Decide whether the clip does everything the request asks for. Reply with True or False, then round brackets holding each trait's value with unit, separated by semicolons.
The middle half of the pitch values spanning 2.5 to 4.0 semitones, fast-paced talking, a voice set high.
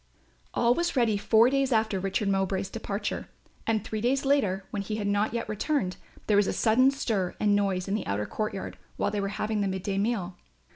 True (2.8 semitones; 210 wpm; 210 Hz)